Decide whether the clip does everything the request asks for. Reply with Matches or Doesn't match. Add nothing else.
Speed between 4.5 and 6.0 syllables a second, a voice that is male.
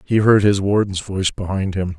Matches